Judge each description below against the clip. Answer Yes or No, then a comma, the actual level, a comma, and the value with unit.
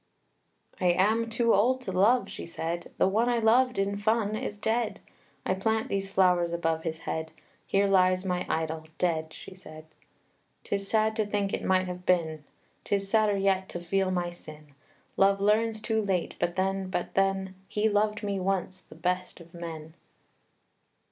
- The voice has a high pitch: Yes, high, 195 Hz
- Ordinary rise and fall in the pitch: Yes, average, 3.2 semitones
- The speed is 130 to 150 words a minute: No, average, 175 wpm